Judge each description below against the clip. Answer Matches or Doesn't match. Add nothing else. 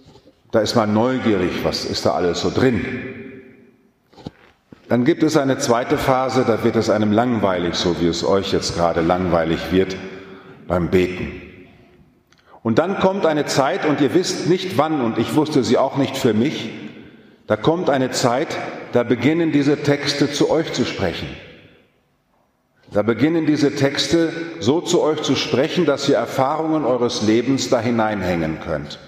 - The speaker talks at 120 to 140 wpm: Doesn't match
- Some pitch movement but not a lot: Doesn't match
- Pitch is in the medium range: Doesn't match